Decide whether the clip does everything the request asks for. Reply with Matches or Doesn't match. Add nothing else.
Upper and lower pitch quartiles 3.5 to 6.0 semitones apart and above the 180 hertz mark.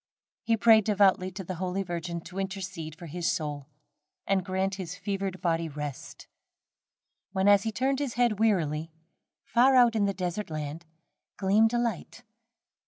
Matches